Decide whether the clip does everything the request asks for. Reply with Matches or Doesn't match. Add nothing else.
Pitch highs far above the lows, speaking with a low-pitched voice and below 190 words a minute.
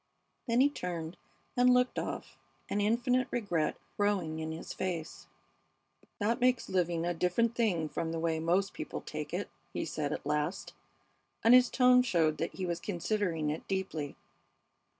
Doesn't match